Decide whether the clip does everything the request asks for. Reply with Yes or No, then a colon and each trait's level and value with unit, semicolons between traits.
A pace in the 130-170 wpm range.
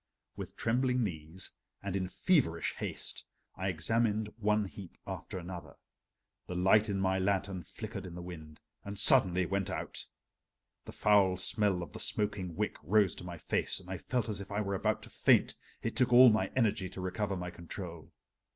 No: average, 180 wpm